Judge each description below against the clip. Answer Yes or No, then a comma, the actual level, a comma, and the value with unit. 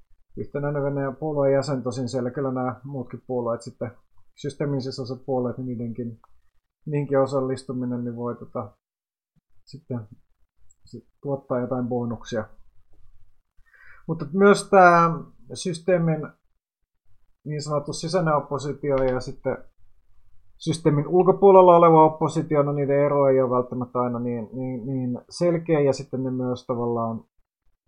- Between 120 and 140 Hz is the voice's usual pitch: Yes, low, 130 Hz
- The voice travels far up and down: No, average, 3.5 semitones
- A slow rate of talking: No, average, 120 wpm